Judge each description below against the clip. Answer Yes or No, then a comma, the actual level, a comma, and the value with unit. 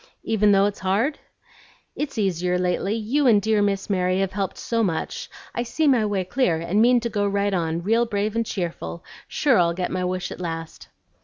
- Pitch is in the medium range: No, high, 200 Hz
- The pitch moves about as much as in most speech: Yes, average, 3.7 semitones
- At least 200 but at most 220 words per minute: Yes, fast, 205 wpm